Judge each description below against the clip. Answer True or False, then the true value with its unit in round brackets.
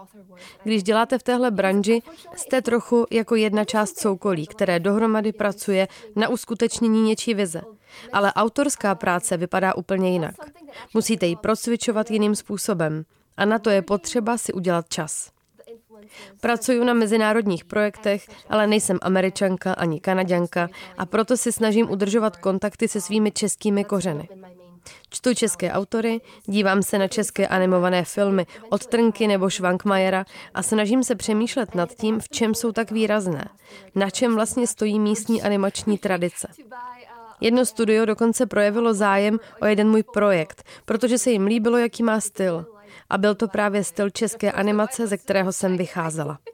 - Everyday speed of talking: True (145 wpm)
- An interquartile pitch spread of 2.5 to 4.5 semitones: True (2.9 semitones)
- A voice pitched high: True (210 Hz)